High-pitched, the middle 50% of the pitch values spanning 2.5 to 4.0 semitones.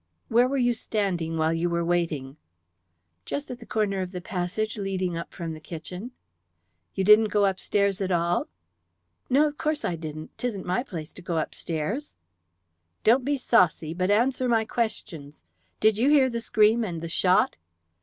No: high, 195 Hz; wide, 5.4 semitones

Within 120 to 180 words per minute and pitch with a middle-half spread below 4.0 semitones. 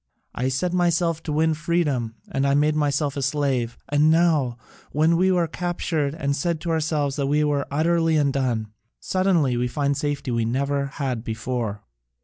Yes: average, 175 wpm; average, 3.3 semitones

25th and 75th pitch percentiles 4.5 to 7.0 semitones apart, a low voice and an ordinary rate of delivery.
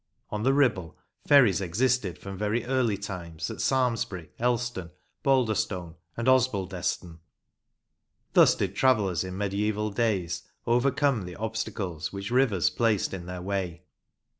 No: average, 4.8 semitones; low, 100 Hz; slow, 125 wpm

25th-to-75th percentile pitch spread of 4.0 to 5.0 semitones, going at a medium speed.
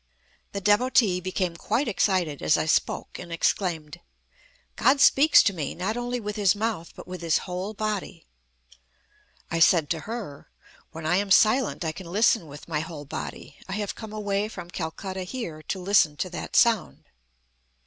Yes: average, 4.3 semitones; average, 170 wpm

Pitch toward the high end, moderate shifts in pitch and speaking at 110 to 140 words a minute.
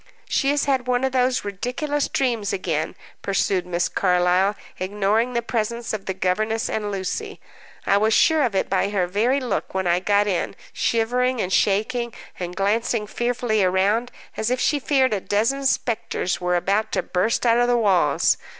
No: high, 215 Hz; average, 4.4 semitones; average, 175 wpm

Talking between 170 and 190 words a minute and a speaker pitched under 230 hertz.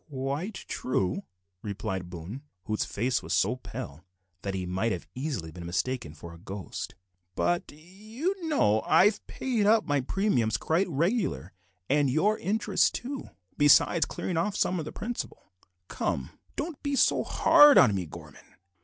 No: average, 155 wpm; medium, 140 Hz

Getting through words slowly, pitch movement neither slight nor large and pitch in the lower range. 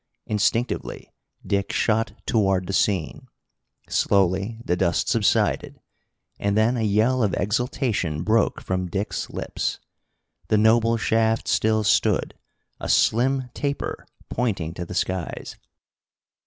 Yes: slow, 115 wpm; average, 3.3 semitones; low, 105 Hz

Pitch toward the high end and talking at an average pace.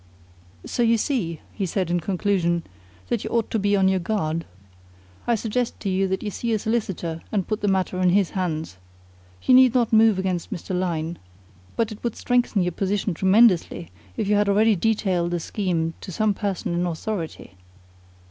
Yes: high, 195 Hz; average, 185 wpm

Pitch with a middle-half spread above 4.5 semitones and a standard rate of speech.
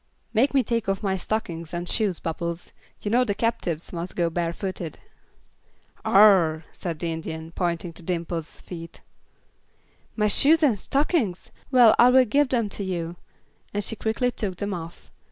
Yes: average, 5.0 semitones; average, 160 wpm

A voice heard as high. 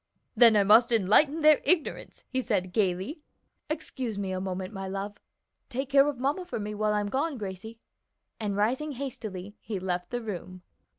Yes: high, 215 Hz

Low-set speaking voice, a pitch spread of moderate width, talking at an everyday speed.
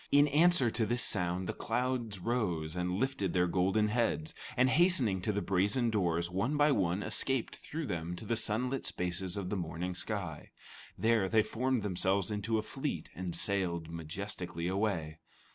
Yes: low, 100 Hz; average, 4.8 semitones; average, 170 wpm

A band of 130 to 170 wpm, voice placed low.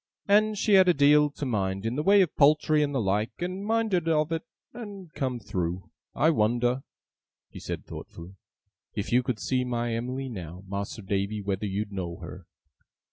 No: average, 185 wpm; low, 125 Hz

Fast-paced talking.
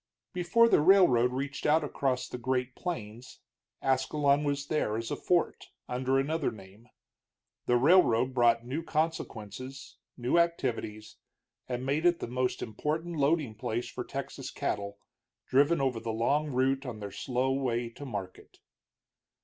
No: average, 145 wpm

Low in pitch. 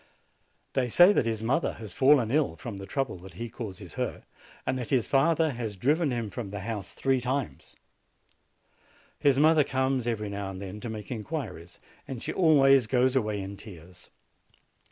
Yes: low, 120 Hz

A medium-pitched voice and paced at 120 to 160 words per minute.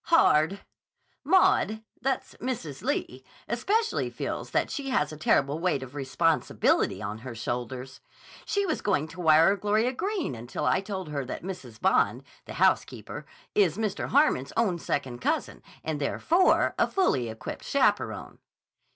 Yes: medium, 170 Hz; average, 140 wpm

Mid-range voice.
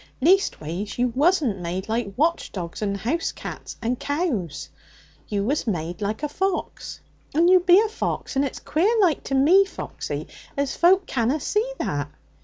No: very high, 275 Hz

